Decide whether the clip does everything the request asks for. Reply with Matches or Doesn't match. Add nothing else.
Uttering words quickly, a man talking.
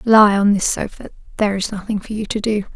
Doesn't match